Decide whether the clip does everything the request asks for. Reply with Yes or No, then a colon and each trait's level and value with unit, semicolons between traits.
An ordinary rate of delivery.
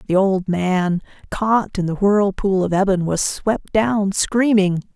Yes: average, 155 wpm